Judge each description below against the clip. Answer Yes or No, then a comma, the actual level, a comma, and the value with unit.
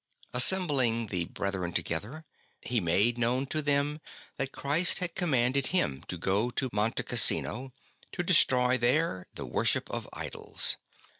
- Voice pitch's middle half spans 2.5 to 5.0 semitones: No, wide, 5.5 semitones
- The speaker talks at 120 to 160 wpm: Yes, average, 140 wpm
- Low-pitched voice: Yes, low, 125 Hz